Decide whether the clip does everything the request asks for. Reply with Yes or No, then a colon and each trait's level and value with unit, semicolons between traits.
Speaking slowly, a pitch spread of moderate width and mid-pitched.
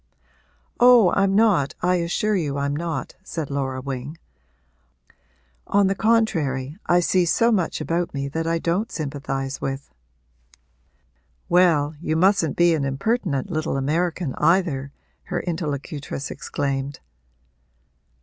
Yes: slow, 120 wpm; average, 4.6 semitones; medium, 165 Hz